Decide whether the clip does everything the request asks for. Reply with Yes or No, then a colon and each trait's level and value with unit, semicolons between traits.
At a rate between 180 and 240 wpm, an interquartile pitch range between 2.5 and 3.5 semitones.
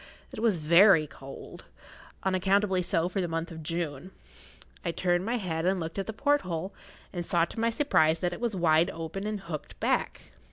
Yes: average, 185 wpm; average, 3.2 semitones